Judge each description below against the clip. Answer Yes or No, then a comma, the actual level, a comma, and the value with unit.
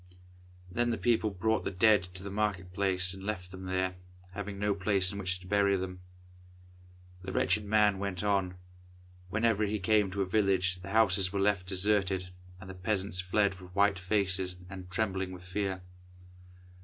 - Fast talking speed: No, average, 175 wpm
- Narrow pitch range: Yes, narrow, 2.0 semitones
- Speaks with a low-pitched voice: Yes, very low, 95 Hz